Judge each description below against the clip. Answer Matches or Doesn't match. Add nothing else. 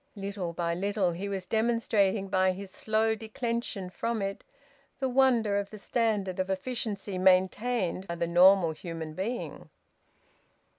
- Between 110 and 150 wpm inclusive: Matches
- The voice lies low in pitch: Doesn't match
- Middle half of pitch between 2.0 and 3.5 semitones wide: Matches